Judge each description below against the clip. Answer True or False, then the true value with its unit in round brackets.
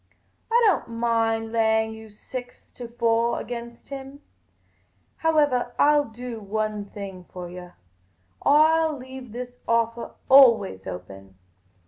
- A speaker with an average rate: False (125 wpm)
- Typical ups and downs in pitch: True (3.3 semitones)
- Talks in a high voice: True (230 Hz)